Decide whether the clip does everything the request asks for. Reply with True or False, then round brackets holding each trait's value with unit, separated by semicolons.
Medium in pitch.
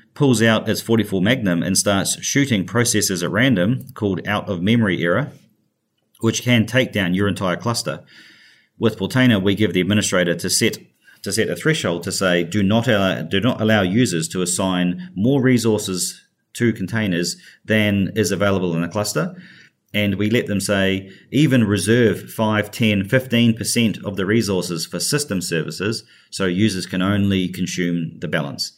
False (105 Hz)